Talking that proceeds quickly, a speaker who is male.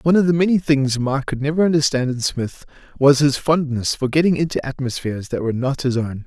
Yes: fast, 230 wpm; male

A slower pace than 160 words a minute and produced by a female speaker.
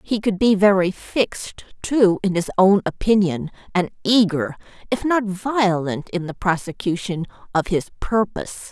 Yes: average, 145 wpm; female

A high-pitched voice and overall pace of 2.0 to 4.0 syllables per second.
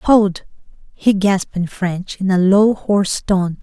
Yes: high, 195 Hz; 3.9 syllables/s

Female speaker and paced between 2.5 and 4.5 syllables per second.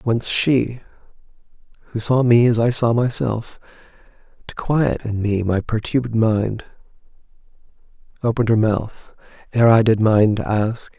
No: male; 4.4 syllables/s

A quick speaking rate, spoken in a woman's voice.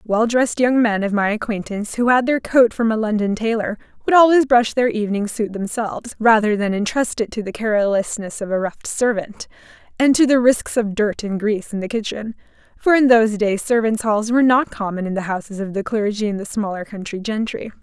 Yes: fast, 215 wpm; female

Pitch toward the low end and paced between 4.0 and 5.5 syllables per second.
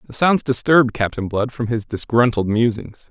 Yes: low, 115 Hz; 5.1 syllables/s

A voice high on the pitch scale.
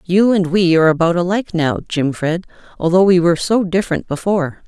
No: medium, 175 Hz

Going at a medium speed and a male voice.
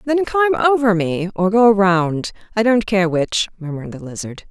No: average, 160 wpm; female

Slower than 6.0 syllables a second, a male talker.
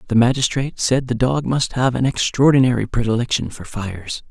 Yes: 5.7 syllables/s; male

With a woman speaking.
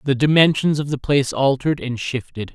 No: male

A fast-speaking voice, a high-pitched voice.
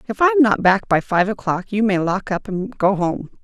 Yes: fast, 260 wpm; high, 205 Hz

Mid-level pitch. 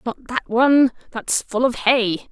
No: high, 240 Hz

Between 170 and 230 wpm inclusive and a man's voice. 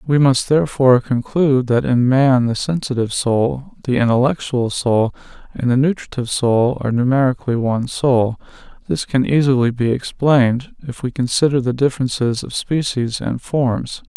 No: average, 150 wpm; male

